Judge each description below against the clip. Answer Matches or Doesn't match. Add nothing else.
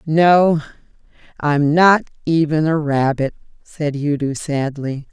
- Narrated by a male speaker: Doesn't match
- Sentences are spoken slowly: Matches